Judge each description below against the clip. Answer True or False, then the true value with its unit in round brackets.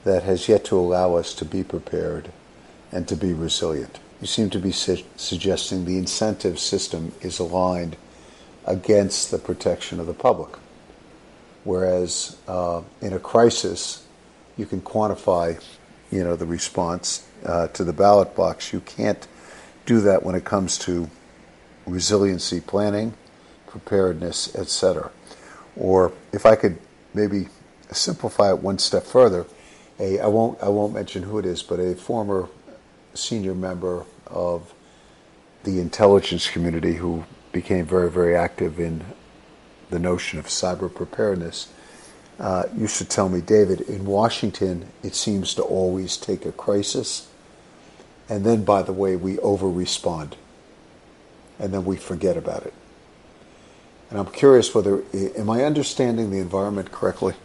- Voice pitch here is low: True (95 Hz)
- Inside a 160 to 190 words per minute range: False (145 wpm)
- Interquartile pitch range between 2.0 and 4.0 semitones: True (2.6 semitones)